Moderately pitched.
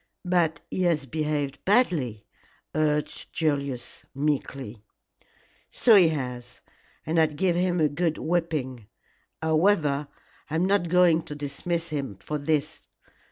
Yes: medium, 155 Hz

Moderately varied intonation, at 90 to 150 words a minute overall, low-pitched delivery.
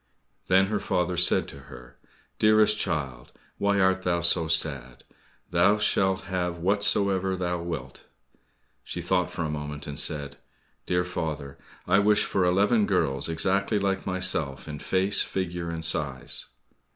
Yes: average, 3.8 semitones; average, 145 wpm; very low, 90 Hz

